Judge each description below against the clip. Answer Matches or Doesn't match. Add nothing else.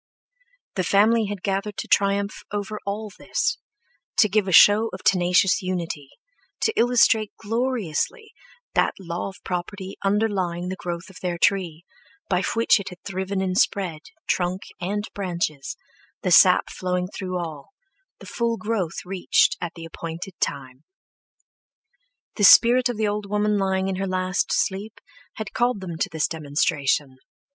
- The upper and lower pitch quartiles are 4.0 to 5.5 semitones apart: Doesn't match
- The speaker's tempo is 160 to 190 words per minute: Doesn't match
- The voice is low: Doesn't match